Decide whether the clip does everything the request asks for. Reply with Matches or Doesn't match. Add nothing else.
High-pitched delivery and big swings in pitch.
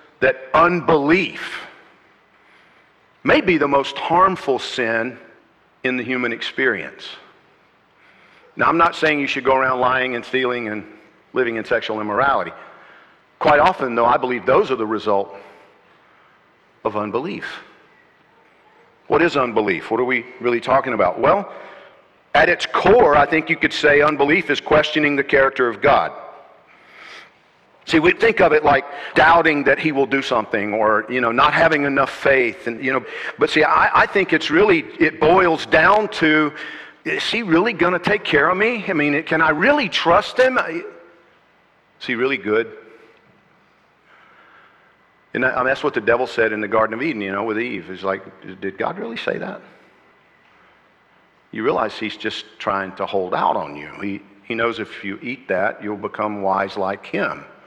Doesn't match